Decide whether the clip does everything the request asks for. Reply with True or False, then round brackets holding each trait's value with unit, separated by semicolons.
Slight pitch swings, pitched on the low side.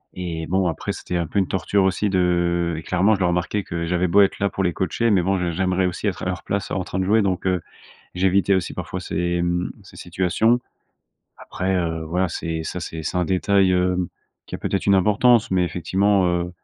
True (1.7 semitones; 90 Hz)